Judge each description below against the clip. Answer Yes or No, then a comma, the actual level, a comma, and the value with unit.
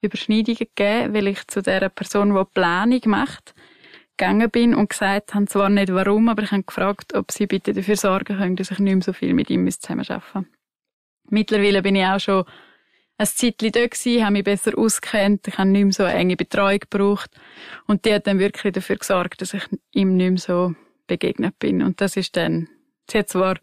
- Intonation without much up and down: Yes, narrow, 1.8 semitones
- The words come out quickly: Yes, fast, 200 wpm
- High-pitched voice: Yes, high, 200 Hz